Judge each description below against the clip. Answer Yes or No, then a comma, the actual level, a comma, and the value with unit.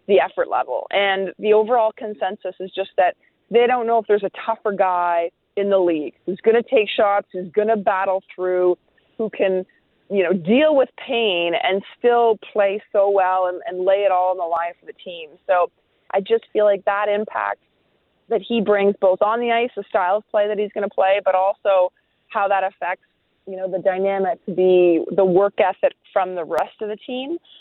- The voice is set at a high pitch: Yes, high, 195 Hz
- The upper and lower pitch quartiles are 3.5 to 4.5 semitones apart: No, average, 2.9 semitones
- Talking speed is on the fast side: Yes, fast, 210 wpm